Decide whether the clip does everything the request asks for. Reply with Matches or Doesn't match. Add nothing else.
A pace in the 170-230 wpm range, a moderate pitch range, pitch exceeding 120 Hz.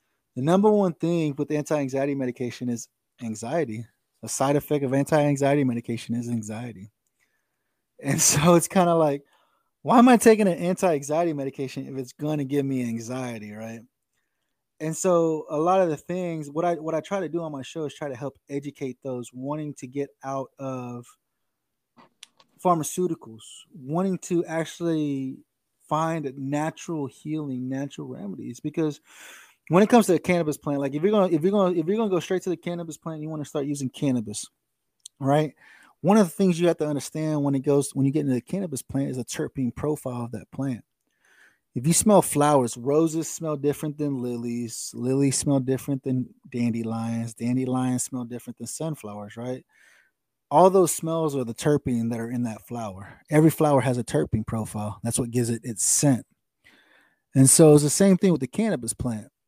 Matches